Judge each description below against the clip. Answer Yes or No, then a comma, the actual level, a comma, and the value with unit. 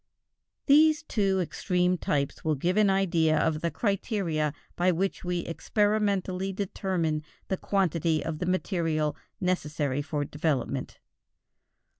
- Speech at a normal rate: No, slow, 120 wpm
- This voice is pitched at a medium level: Yes, medium, 180 Hz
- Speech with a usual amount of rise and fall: Yes, average, 3.8 semitones